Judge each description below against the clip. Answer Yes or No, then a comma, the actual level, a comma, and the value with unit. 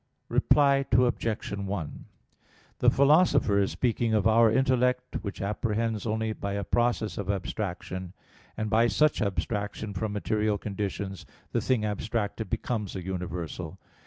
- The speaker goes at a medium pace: No, slow, 130 wpm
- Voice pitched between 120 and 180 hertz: No, low, 110 Hz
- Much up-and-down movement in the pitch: No, average, 2.8 semitones